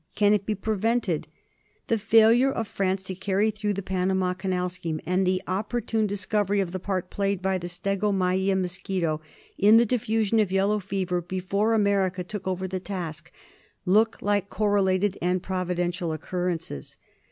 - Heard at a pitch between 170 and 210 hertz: Yes, high, 190 Hz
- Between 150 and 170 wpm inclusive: Yes, average, 155 wpm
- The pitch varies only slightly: Yes, narrow, 2.2 semitones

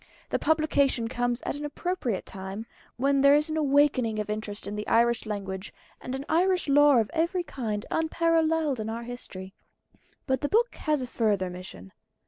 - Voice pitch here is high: Yes, very high, 255 Hz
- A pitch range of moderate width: No, wide, 6.0 semitones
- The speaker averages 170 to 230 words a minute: Yes, average, 175 wpm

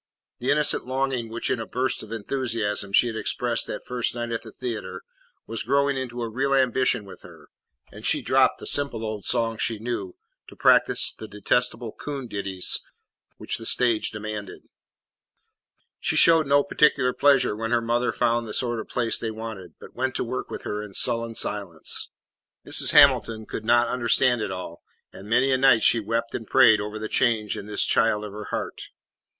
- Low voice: Yes, low, 115 Hz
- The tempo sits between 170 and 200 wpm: Yes, average, 190 wpm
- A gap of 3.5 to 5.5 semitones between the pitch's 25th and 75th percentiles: No, average, 2.7 semitones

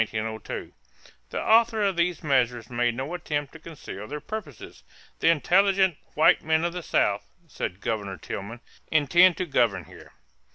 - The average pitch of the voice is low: No, medium, 150 Hz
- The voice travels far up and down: Yes, wide, 7.0 semitones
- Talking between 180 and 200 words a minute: No, average, 150 wpm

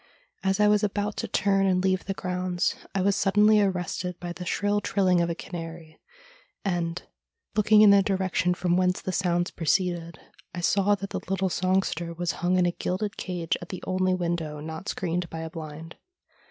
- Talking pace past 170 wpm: Yes, average, 190 wpm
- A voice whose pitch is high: No, medium, 180 Hz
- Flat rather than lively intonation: Yes, narrow, 2.1 semitones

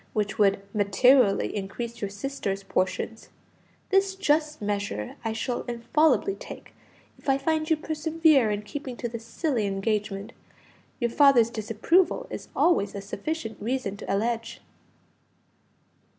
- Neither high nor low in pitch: No, high, 230 Hz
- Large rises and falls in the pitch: Yes, wide, 6.4 semitones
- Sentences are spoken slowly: Yes, slow, 130 wpm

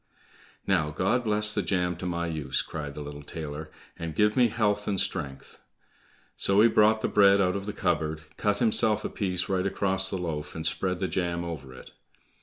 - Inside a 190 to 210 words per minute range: Yes, average, 200 wpm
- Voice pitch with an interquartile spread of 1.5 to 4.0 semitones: No, average, 4.5 semitones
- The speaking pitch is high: No, very low, 90 Hz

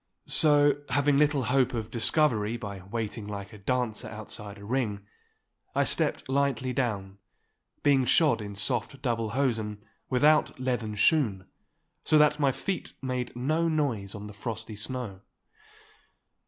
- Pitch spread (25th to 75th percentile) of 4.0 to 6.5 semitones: Yes, average, 4.7 semitones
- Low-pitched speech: Yes, low, 120 Hz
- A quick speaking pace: No, average, 140 wpm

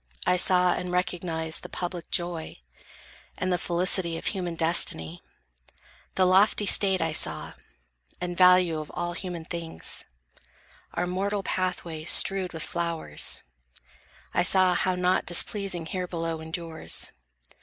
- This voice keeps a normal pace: No, slow, 130 wpm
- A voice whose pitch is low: No, medium, 175 Hz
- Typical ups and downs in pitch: No, narrow, 1.8 semitones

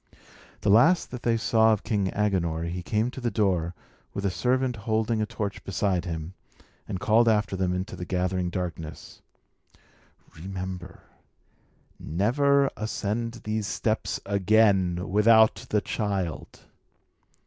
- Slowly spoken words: Yes, slow, 130 wpm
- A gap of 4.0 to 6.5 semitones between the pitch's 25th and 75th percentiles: No, average, 3.4 semitones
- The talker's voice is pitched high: No, low, 100 Hz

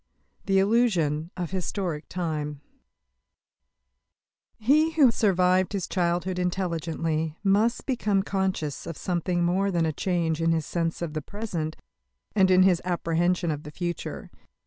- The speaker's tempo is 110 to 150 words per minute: Yes, average, 140 wpm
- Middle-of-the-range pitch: Yes, medium, 180 Hz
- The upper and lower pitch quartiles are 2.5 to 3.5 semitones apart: Yes, average, 2.8 semitones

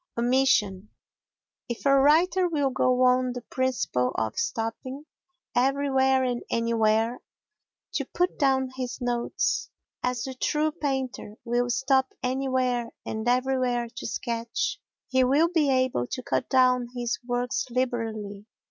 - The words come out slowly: Yes, slow, 130 wpm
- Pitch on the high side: Yes, very high, 255 Hz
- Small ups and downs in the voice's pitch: Yes, narrow, 2.0 semitones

